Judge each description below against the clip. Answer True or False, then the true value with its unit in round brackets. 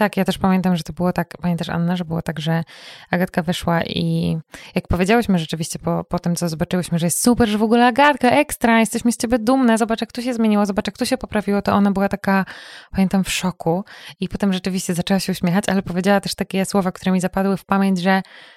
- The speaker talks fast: True (230 wpm)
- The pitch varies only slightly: False (3.2 semitones)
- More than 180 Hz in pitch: True (190 Hz)